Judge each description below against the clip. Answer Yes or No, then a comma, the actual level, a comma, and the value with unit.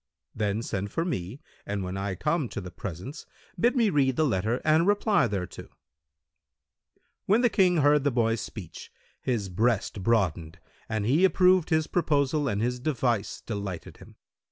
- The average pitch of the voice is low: Yes, low, 120 Hz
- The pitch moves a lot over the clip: Yes, wide, 7.5 semitones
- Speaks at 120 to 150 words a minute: No, average, 160 wpm